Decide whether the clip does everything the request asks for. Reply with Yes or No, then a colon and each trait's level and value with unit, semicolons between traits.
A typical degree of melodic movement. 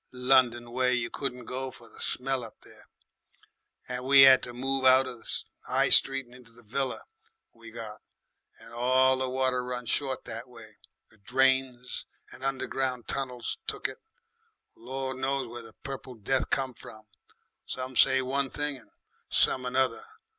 No: narrow, 1.6 semitones